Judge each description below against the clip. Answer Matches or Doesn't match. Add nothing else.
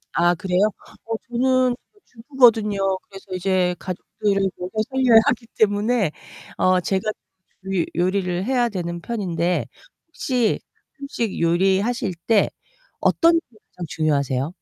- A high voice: Matches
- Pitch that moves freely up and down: Doesn't match